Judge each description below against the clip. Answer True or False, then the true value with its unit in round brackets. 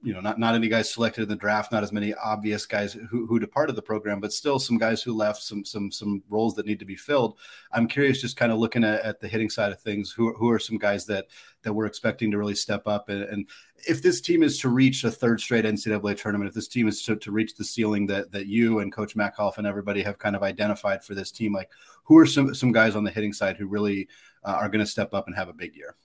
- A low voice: True (105 Hz)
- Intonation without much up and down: True (1.8 semitones)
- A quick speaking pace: True (280 wpm)